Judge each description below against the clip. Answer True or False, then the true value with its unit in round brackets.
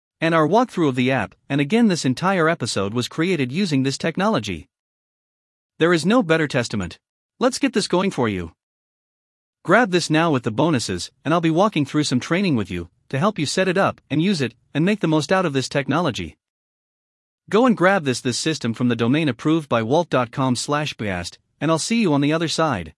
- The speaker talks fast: True (210 wpm)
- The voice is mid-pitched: True (150 Hz)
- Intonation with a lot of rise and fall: True (6.0 semitones)